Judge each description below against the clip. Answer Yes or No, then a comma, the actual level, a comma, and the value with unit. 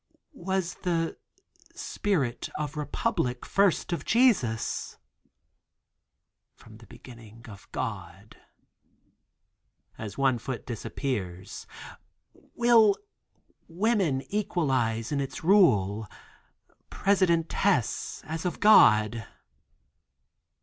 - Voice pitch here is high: No, medium, 140 Hz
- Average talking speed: No, slow, 80 wpm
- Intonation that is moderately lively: No, wide, 8.7 semitones